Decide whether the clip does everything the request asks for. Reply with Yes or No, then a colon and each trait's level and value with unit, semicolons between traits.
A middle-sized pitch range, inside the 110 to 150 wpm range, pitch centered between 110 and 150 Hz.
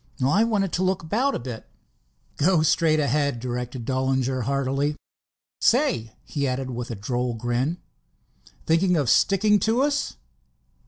No: wide, 6.4 semitones; average, 140 wpm; medium, 140 Hz